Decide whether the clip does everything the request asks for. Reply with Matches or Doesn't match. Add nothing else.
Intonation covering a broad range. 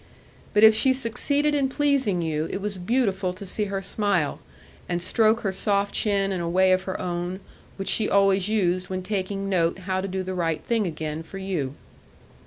Doesn't match